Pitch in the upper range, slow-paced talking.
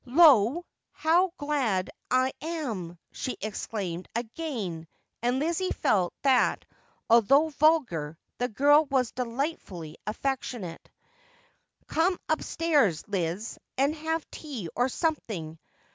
Yes: very high, 255 Hz; slow, 110 wpm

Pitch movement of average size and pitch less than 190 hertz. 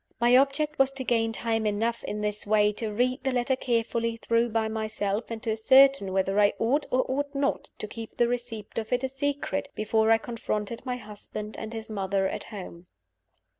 No: average, 3.0 semitones; high, 225 Hz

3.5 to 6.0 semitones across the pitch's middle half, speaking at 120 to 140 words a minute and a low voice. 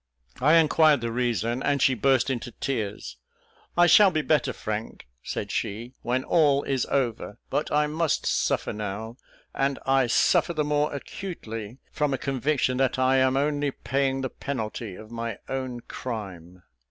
No: average, 3.9 semitones; average, 160 wpm; low, 130 Hz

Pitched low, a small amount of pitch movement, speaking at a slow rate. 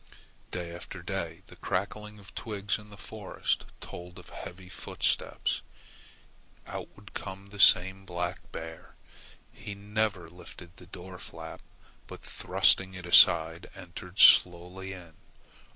Yes: very low, 95 Hz; narrow, 2.3 semitones; slow, 130 wpm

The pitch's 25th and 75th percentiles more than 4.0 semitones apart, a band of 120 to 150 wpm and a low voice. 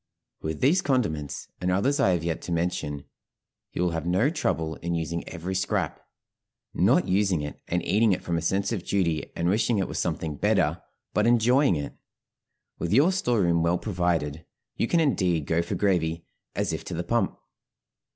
No: average, 4.4 semitones; average, 185 wpm; very low, 90 Hz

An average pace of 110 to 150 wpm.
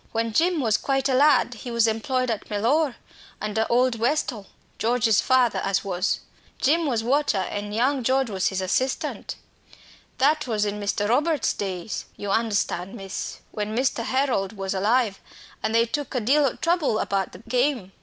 No: average, 170 wpm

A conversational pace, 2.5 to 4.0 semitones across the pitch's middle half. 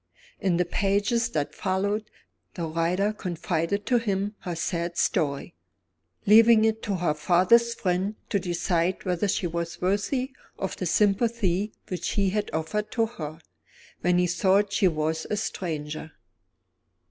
Yes: average, 145 wpm; average, 3.5 semitones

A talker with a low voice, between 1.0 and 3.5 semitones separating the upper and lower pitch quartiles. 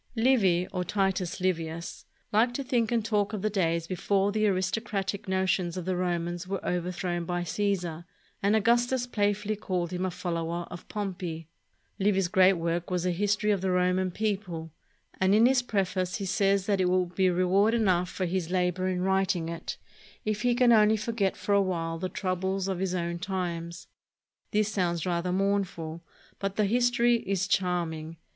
No: medium, 185 Hz; narrow, 2.6 semitones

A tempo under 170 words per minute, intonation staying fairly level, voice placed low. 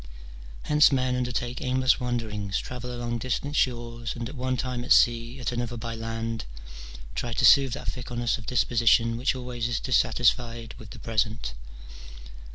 Yes: average, 160 wpm; narrow, 1.5 semitones; low, 120 Hz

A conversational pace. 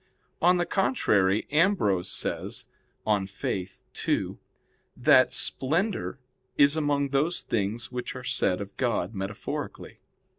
No: slow, 115 wpm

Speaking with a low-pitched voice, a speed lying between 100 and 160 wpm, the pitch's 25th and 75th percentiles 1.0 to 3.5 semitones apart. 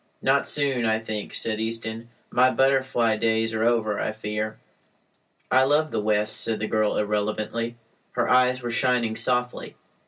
Yes: low, 115 Hz; average, 155 wpm; narrow, 2.5 semitones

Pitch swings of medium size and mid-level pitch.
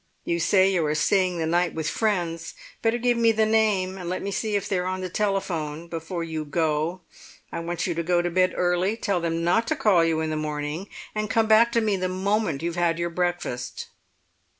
Yes: average, 3.3 semitones; medium, 180 Hz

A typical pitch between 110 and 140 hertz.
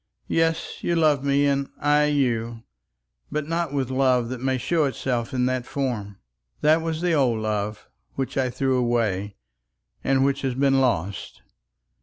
Yes: low, 135 Hz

